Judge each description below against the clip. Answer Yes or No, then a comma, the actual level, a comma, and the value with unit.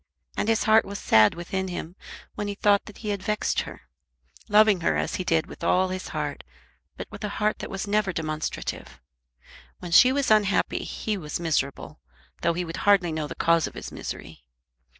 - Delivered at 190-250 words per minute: Yes, average, 195 wpm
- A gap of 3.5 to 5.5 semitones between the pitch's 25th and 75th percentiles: Yes, average, 4.2 semitones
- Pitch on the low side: No, medium, 185 Hz